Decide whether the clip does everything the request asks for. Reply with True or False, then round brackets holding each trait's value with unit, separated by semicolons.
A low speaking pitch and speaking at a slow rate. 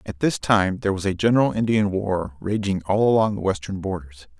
False (100 Hz; 205 wpm)